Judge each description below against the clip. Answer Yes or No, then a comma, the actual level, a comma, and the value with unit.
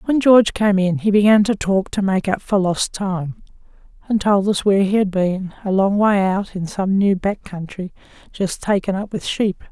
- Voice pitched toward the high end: Yes, high, 195 Hz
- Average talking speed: No, fast, 210 wpm